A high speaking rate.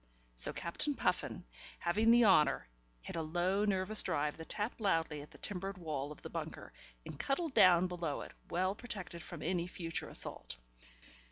No: average, 170 wpm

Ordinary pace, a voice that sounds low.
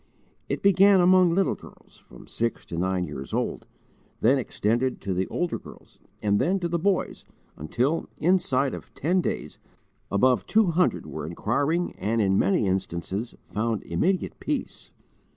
Yes: average, 150 wpm; low, 130 Hz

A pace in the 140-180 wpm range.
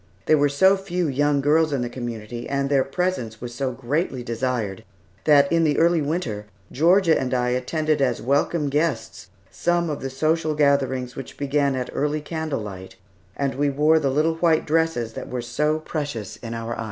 No: average, 190 wpm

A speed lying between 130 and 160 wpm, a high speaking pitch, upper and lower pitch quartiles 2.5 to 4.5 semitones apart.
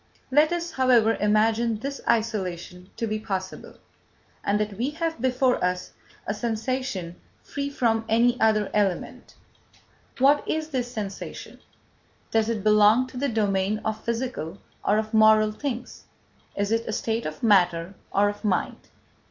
Yes: average, 145 wpm; high, 220 Hz; average, 3.3 semitones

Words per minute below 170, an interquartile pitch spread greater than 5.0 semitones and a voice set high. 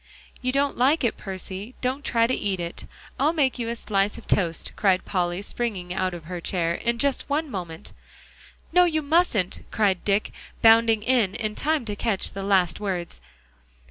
No: average, 180 wpm; wide, 5.5 semitones; high, 210 Hz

